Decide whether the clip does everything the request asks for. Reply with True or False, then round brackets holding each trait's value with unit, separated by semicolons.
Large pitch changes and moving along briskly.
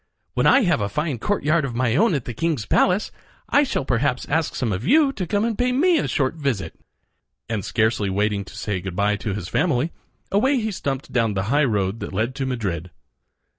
True (8.6 semitones; 215 wpm)